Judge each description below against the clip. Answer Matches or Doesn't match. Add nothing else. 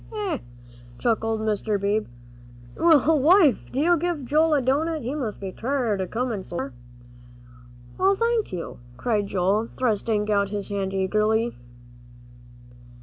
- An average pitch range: Doesn't match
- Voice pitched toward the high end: Matches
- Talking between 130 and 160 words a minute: Matches